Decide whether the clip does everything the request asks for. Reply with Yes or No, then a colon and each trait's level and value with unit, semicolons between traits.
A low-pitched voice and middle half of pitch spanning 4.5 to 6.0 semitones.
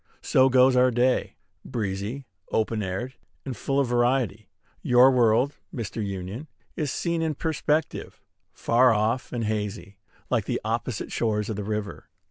No: low, 120 Hz; average, 3.6 semitones